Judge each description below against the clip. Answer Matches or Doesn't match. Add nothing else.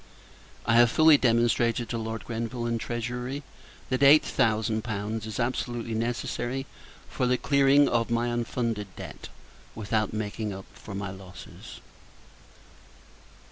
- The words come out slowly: Matches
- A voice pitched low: Matches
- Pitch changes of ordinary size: Doesn't match